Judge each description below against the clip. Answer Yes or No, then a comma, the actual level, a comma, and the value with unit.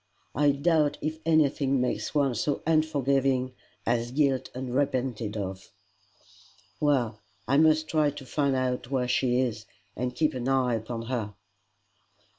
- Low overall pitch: Yes, low, 130 Hz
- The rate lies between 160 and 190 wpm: No, slow, 135 wpm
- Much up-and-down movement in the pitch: No, average, 3.0 semitones